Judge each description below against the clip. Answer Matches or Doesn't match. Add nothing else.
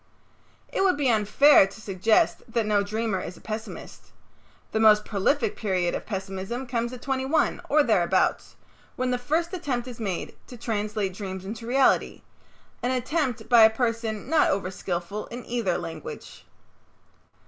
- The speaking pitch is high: Matches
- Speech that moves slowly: Doesn't match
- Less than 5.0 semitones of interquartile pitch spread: Matches